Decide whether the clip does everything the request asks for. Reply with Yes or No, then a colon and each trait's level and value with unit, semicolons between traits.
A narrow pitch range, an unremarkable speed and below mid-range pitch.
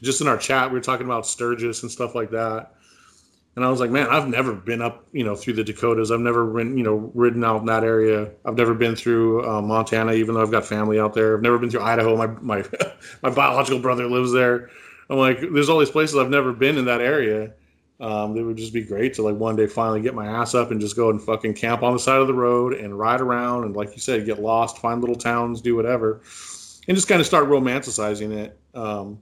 No: narrow, 2.0 semitones; fast, 255 wpm; low, 115 Hz